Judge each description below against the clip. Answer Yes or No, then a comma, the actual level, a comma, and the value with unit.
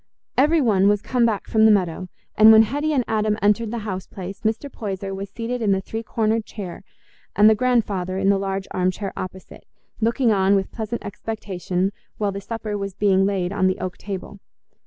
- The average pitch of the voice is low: No, high, 205 Hz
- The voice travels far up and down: No, narrow, 2.5 semitones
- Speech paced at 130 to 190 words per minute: No, average, 200 wpm